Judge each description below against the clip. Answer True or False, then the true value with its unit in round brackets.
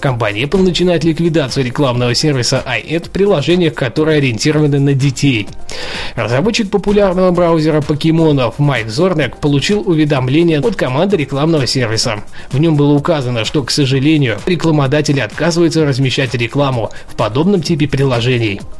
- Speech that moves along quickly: False (130 wpm)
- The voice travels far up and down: False (3.5 semitones)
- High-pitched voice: False (150 Hz)